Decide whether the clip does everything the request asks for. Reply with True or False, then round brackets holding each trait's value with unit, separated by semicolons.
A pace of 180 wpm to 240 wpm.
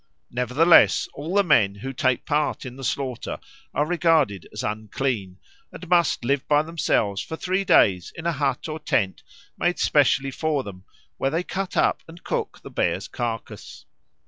False (170 wpm)